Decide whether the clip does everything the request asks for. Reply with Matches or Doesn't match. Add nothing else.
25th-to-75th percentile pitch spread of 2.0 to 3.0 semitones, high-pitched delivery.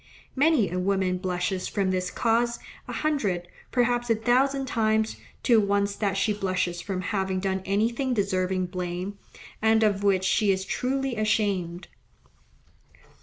Doesn't match